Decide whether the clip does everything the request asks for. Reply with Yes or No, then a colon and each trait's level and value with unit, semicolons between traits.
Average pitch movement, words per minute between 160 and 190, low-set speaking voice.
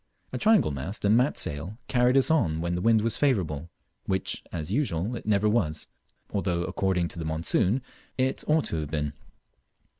No: wide, 7.1 semitones; average, 180 wpm; very low, 95 Hz